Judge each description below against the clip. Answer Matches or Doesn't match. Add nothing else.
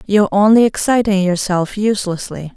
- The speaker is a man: Doesn't match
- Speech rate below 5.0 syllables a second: Doesn't match